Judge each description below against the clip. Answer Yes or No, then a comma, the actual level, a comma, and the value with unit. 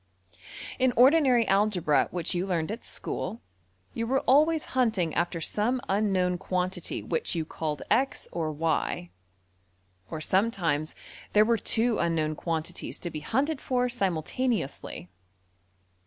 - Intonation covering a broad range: Yes, wide, 6.8 semitones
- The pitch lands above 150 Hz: Yes, high, 190 Hz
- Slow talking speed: Yes, slow, 125 wpm